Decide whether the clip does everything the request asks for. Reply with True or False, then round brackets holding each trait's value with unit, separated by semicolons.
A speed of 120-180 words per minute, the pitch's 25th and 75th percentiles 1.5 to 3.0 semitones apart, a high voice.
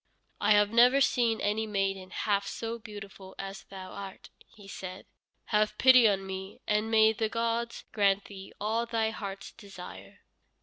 True (160 wpm; 2.5 semitones; 210 Hz)